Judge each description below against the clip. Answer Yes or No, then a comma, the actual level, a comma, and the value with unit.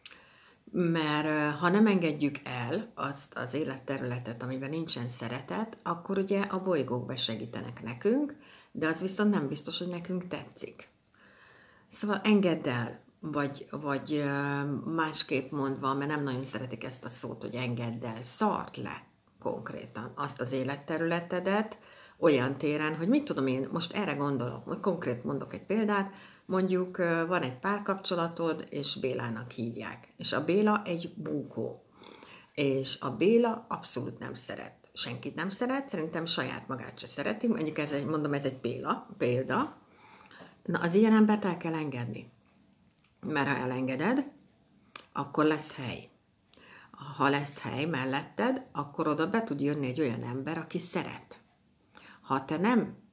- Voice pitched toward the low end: No, medium, 155 Hz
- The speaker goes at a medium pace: Yes, average, 140 wpm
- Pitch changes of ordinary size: No, wide, 5.9 semitones